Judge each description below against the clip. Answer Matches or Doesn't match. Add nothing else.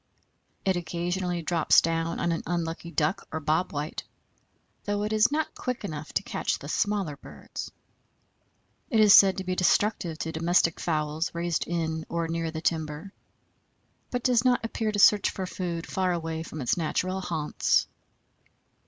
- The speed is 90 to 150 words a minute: Doesn't match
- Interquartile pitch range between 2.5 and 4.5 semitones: Matches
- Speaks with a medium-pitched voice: Matches